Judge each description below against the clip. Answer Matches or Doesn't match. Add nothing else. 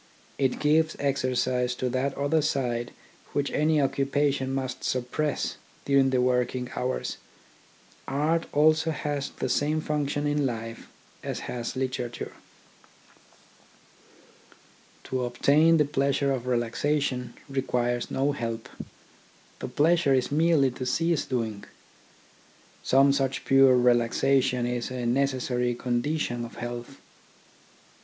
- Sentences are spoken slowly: Matches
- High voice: Doesn't match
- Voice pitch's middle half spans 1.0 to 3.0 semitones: Matches